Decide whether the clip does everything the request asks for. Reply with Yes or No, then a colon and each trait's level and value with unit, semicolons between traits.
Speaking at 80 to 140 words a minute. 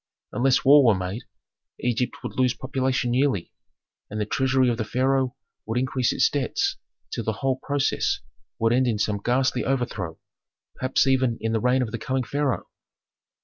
No: average, 170 wpm